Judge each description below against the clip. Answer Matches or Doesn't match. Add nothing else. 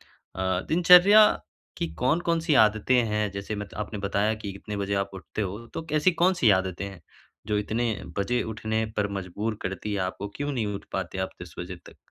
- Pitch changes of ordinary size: Matches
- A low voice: Matches